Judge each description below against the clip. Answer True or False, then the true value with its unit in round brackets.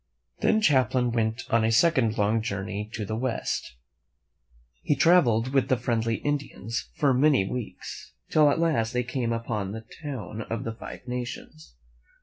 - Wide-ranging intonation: False (3.1 semitones)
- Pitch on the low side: True (115 Hz)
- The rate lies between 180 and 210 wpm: False (155 wpm)